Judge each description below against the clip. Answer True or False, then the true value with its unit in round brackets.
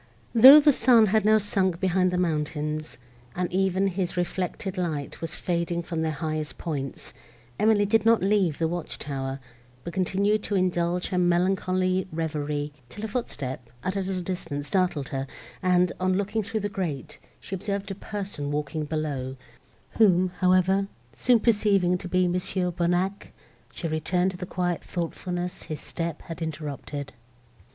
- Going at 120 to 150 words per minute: False (160 wpm)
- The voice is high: False (180 Hz)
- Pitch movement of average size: True (3.4 semitones)